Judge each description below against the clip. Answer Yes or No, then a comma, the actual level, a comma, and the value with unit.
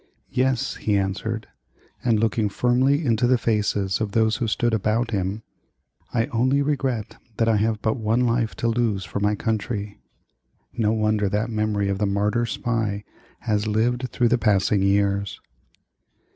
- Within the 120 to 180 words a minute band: Yes, average, 160 wpm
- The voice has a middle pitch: No, low, 110 Hz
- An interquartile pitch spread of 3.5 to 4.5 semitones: No, narrow, 2.4 semitones